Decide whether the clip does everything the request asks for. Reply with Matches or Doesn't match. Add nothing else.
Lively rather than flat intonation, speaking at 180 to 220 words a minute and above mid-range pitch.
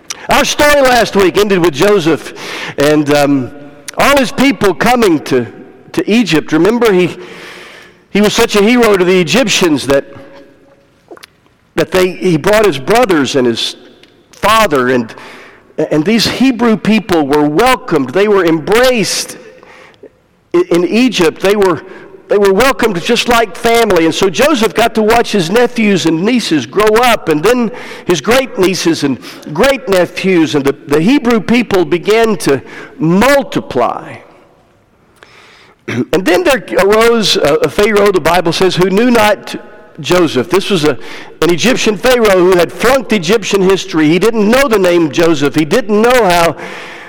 Doesn't match